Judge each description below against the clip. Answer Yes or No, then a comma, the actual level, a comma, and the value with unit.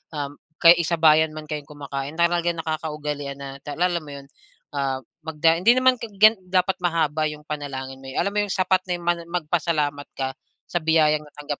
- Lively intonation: No, average, 3.1 semitones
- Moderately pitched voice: Yes, medium, 155 Hz